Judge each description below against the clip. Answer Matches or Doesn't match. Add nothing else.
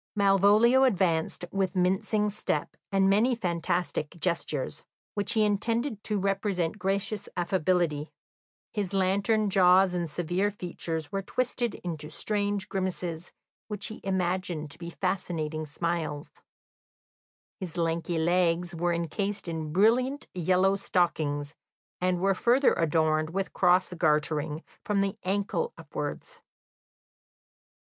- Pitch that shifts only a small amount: Doesn't match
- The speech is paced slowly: Matches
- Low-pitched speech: Doesn't match